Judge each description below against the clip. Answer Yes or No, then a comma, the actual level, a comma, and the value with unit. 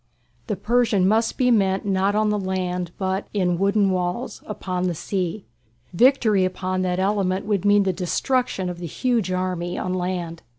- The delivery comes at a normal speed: Yes, average, 170 wpm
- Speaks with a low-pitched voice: No, high, 190 Hz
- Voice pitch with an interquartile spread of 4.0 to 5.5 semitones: No, narrow, 2.4 semitones